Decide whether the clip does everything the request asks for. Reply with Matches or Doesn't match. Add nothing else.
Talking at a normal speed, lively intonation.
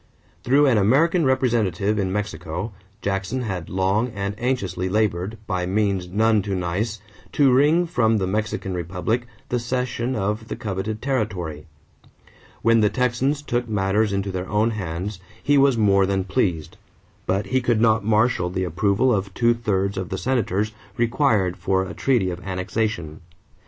Doesn't match